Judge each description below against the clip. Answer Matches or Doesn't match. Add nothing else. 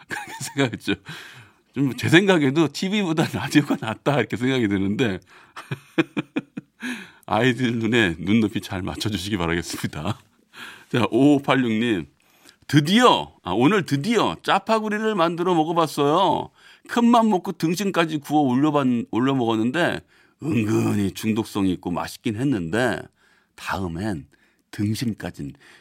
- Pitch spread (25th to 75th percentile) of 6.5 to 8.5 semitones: Matches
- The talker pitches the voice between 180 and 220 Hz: Doesn't match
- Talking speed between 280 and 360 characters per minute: Doesn't match